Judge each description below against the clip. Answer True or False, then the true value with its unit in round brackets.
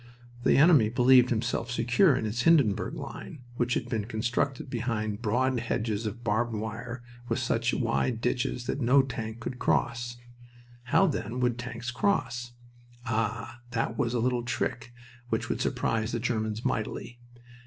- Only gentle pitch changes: True (1.6 semitones)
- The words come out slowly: False (155 wpm)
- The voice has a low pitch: True (120 Hz)